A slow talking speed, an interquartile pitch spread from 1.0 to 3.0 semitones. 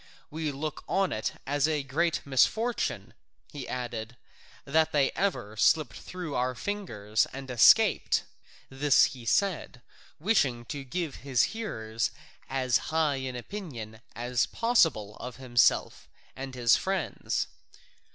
No: slow, 125 wpm; average, 5.0 semitones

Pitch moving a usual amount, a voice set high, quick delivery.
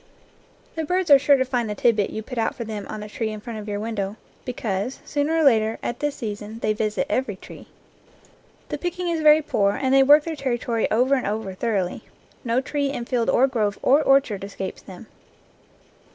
Yes: average, 4.6 semitones; high, 235 Hz; fast, 210 wpm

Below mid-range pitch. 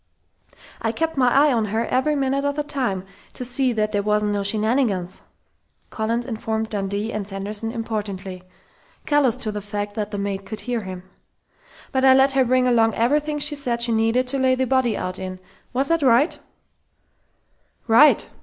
No: high, 230 Hz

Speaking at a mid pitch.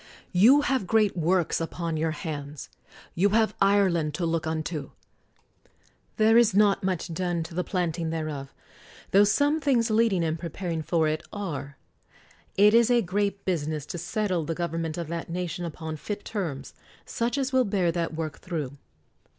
Yes: medium, 175 Hz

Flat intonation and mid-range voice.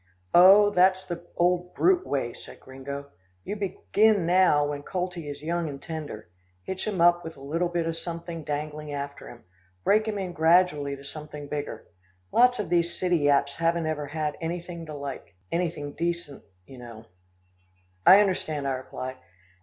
No: average, 3.7 semitones; medium, 165 Hz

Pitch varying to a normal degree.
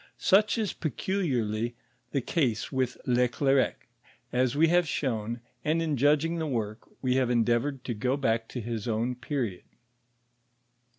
Yes: average, 4.1 semitones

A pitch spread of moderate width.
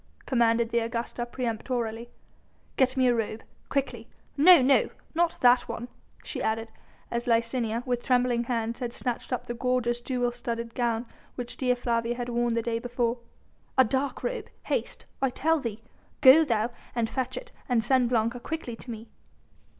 No: narrow, 1.6 semitones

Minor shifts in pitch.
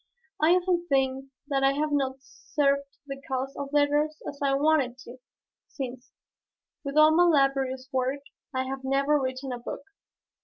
Yes: narrow, 1.8 semitones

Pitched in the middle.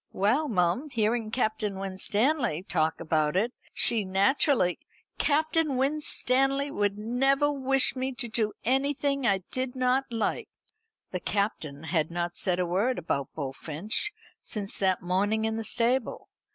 No: high, 220 Hz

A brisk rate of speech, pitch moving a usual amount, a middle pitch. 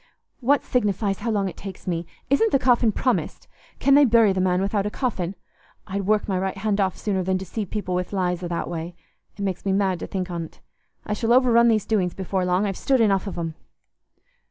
No: fast, 220 wpm; average, 3.3 semitones; high, 195 Hz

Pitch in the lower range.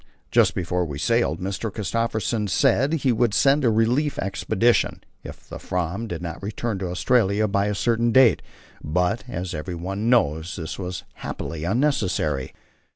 Yes: low, 100 Hz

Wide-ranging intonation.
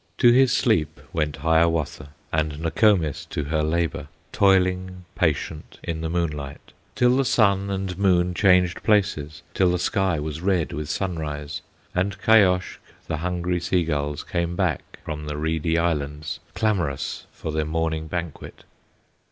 No: average, 3.3 semitones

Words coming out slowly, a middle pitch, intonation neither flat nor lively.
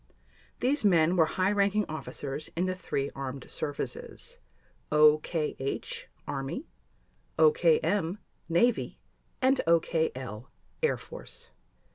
No: slow, 80 wpm; medium, 170 Hz; wide, 8.4 semitones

